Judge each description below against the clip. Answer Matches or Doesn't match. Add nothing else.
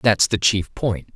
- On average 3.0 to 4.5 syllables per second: Matches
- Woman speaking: Doesn't match